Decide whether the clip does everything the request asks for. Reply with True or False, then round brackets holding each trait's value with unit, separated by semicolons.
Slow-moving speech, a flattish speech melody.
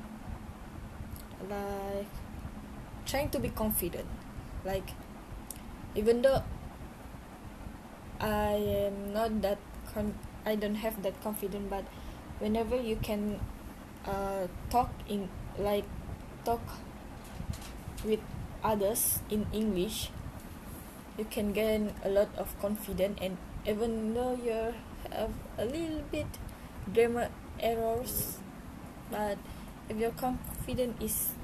True (100 wpm; 2.3 semitones)